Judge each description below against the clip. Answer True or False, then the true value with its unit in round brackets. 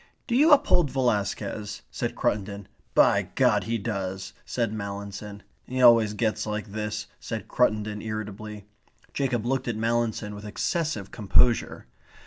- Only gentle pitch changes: True (2.3 semitones)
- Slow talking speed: True (130 wpm)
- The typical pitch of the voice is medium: False (110 Hz)